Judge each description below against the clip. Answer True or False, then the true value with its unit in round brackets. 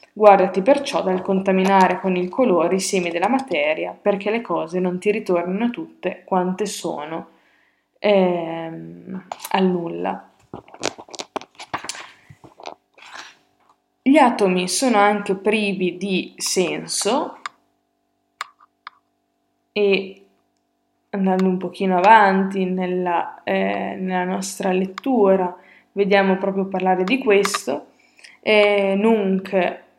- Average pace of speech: False (95 wpm)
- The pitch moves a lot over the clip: False (2.7 semitones)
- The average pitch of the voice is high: True (195 Hz)